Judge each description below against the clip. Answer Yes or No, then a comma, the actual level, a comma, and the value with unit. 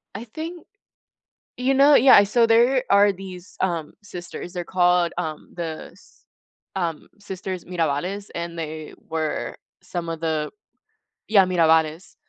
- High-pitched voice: No, medium, 180 Hz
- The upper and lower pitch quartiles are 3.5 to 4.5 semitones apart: Yes, average, 3.9 semitones